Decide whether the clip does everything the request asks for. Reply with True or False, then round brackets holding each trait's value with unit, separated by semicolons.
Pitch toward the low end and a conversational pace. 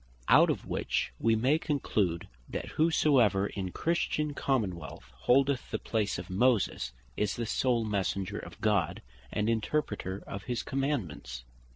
True (110 Hz; 150 wpm)